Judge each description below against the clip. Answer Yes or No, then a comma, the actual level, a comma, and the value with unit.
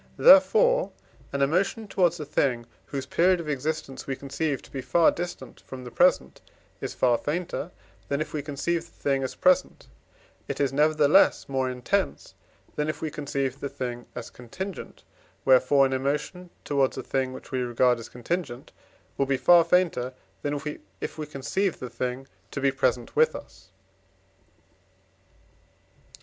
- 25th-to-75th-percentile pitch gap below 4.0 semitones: No, average, 4.3 semitones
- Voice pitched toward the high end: No, medium, 140 Hz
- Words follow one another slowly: No, average, 160 wpm